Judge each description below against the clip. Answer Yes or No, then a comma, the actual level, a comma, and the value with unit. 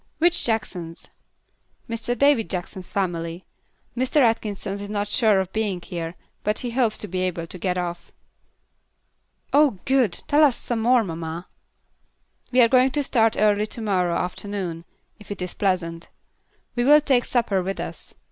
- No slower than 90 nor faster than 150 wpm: No, average, 160 wpm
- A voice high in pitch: Yes, high, 205 Hz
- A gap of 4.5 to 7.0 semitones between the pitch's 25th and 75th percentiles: Yes, average, 5.0 semitones